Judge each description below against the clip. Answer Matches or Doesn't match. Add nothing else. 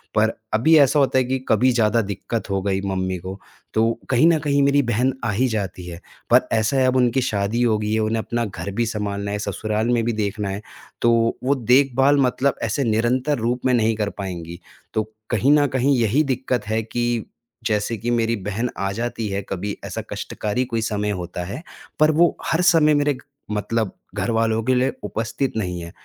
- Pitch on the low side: Matches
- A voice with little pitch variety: Doesn't match